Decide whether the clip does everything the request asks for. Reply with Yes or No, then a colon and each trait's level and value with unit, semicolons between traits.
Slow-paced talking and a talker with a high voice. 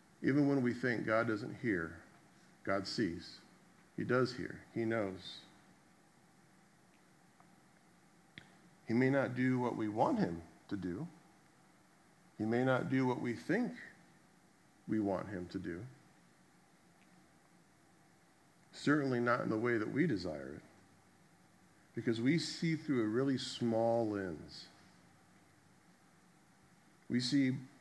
No: slow, 120 wpm; low, 130 Hz